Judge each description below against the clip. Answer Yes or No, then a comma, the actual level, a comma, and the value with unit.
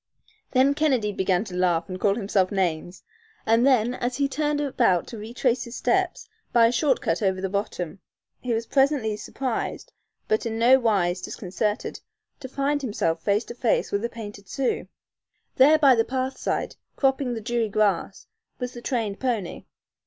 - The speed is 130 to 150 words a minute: No, average, 175 wpm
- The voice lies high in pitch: Yes, high, 230 Hz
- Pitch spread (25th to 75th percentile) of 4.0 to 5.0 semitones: Yes, average, 4.6 semitones